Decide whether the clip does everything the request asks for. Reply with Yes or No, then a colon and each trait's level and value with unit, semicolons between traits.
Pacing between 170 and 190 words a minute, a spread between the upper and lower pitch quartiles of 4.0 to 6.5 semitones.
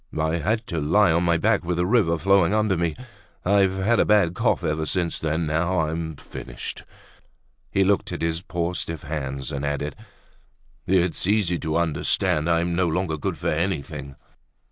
No: average, 175 wpm; average, 3.1 semitones